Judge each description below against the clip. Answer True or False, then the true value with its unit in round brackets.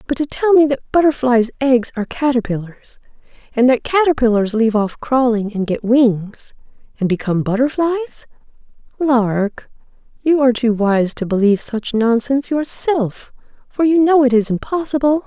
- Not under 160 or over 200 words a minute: False (140 wpm)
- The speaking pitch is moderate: False (250 Hz)